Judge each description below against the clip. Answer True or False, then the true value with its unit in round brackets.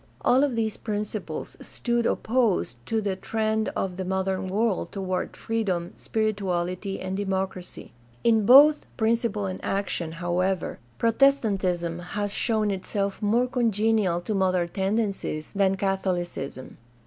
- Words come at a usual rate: False (125 wpm)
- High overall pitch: True (200 Hz)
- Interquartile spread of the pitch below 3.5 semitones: True (3.1 semitones)